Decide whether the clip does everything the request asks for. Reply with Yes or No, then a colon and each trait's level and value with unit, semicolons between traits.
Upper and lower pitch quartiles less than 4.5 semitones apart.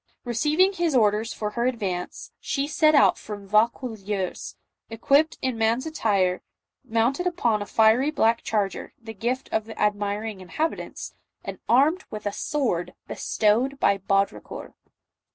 No: average, 4.8 semitones